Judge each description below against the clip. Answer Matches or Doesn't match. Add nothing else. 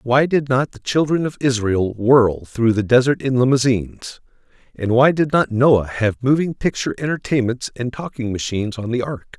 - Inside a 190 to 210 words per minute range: Doesn't match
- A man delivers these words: Matches